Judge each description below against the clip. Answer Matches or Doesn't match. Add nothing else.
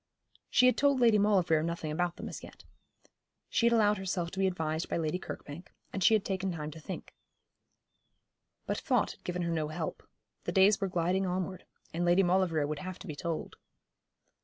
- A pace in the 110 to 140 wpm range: Doesn't match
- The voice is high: Doesn't match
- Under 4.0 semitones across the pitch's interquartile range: Matches